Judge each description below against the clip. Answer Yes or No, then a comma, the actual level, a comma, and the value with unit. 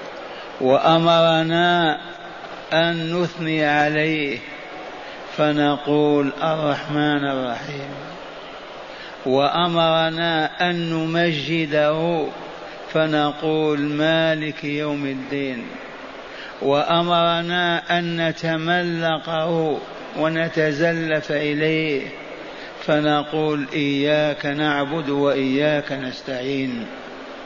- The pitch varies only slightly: Yes, narrow, 2.1 semitones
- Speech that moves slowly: Yes, slow, 50 wpm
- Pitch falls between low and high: Yes, medium, 155 Hz